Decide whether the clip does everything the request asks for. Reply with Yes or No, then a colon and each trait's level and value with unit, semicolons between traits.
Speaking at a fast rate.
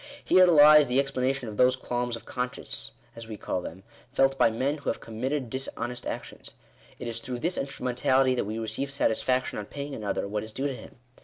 Yes: fast, 210 wpm